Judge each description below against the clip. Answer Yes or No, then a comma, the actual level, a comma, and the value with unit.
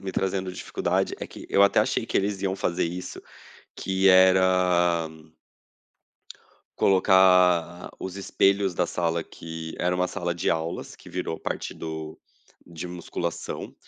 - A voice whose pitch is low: Yes, very low, 90 Hz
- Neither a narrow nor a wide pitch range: No, narrow, 1.9 semitones